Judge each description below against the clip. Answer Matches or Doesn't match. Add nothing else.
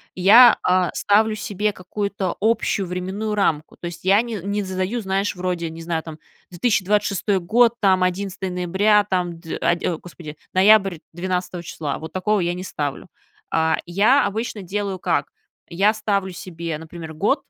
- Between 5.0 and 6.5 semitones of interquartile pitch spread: Doesn't match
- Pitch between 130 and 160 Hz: Doesn't match